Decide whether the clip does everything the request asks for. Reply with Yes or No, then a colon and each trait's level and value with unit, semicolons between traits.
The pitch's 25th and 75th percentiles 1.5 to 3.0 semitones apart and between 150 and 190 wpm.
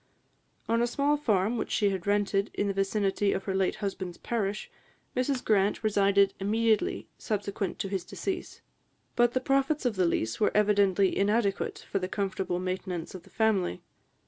Yes: average, 2.7 semitones; average, 170 wpm